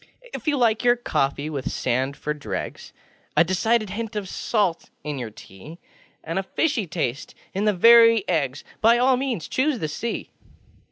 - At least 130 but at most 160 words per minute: No, average, 170 wpm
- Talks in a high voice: Yes, high, 195 Hz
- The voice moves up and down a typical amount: No, wide, 7.7 semitones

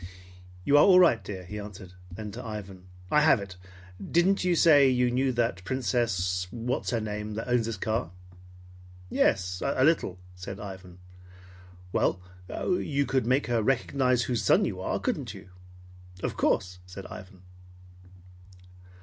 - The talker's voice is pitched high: No, low, 110 Hz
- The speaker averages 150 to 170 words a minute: Yes, average, 155 wpm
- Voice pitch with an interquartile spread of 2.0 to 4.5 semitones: No, wide, 5.5 semitones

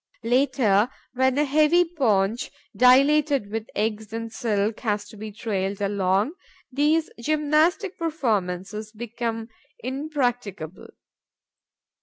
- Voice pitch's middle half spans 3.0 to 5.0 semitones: No, wide, 5.6 semitones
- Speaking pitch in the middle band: No, high, 230 Hz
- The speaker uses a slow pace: Yes, slow, 100 wpm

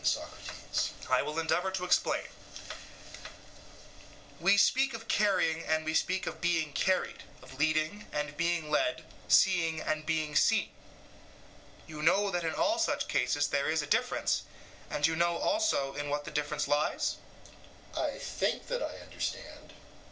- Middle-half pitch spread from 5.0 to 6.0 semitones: No, average, 3.9 semitones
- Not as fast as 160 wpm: Yes, average, 150 wpm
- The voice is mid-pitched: Yes, medium, 160 Hz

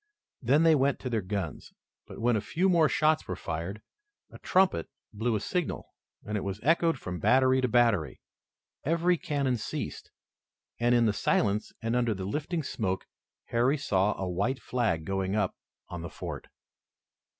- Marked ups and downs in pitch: Yes, wide, 6.3 semitones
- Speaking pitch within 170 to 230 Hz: No, low, 120 Hz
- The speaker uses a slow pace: No, average, 170 wpm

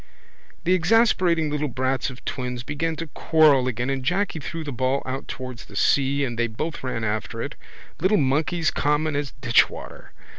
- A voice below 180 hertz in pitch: Yes, medium, 140 Hz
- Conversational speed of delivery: Yes, average, 175 wpm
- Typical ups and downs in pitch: Yes, average, 3.9 semitones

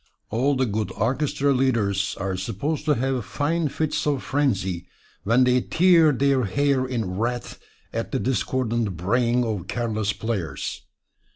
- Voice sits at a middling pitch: No, low, 125 Hz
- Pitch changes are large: No, average, 4.8 semitones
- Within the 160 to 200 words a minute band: No, average, 145 wpm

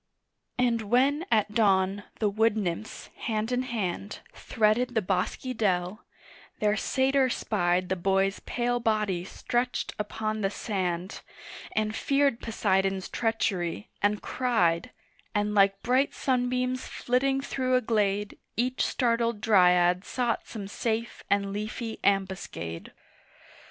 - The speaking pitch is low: No, high, 215 Hz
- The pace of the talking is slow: Yes, slow, 120 wpm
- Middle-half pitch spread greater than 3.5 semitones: Yes, average, 3.9 semitones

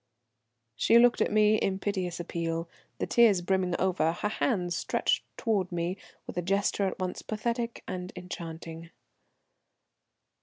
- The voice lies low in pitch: No, medium, 185 Hz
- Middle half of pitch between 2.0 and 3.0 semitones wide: No, average, 3.4 semitones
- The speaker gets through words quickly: No, average, 140 wpm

